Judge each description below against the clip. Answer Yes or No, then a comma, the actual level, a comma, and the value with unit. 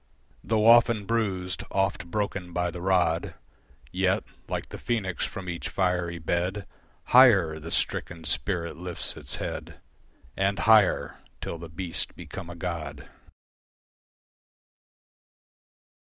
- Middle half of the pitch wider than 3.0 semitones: No, average, 2.7 semitones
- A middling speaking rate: No, slow, 115 wpm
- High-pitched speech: No, very low, 90 Hz